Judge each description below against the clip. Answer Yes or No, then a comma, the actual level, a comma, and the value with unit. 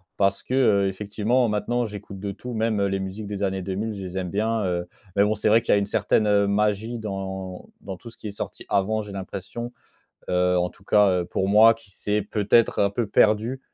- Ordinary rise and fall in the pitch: No, narrow, 2.1 semitones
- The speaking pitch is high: No, low, 100 Hz